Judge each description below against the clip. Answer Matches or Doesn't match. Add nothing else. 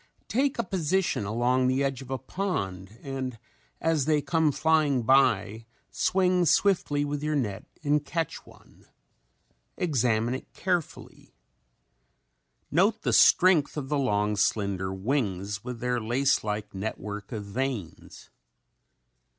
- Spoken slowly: Matches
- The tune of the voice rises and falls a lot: Matches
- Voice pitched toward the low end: Matches